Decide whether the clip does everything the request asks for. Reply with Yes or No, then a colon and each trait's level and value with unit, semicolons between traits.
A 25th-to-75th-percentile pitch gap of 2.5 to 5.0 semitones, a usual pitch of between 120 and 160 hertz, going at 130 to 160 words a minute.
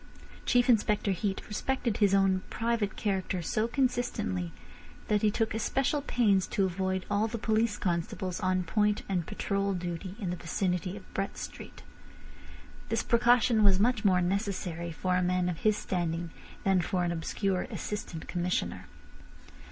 No: average, 3.2 semitones; high, 195 Hz; average, 150 wpm